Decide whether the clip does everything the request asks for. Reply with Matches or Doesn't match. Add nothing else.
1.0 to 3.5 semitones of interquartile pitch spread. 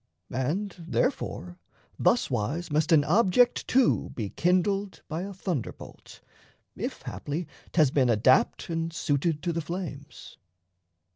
Doesn't match